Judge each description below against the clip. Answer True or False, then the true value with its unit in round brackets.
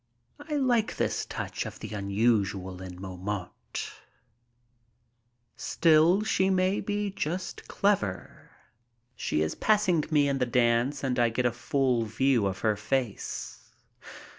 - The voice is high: False (125 Hz)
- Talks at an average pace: False (130 wpm)